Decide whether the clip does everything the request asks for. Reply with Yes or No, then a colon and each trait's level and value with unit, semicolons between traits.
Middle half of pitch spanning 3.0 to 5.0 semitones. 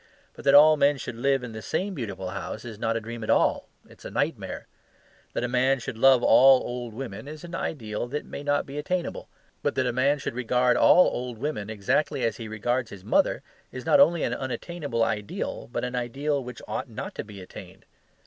Yes: average, 3.8 semitones